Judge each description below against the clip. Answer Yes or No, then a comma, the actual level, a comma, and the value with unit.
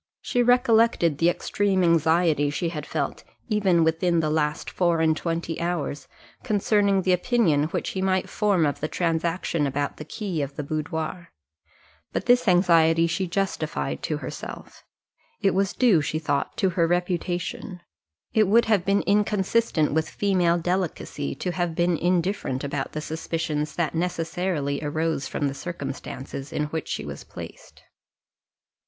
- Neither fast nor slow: Yes, average, 150 wpm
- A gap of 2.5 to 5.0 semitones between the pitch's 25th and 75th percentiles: Yes, average, 3.4 semitones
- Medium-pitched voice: Yes, medium, 170 Hz